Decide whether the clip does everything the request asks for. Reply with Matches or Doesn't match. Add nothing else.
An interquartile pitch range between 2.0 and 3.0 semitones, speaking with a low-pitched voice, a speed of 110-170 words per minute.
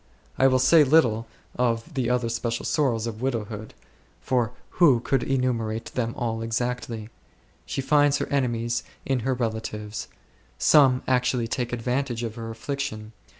Matches